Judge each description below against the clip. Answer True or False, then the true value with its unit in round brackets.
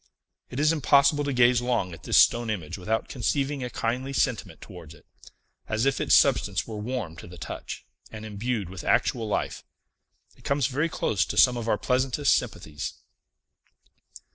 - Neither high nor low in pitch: False (120 Hz)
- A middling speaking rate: True (170 wpm)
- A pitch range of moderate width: True (4.5 semitones)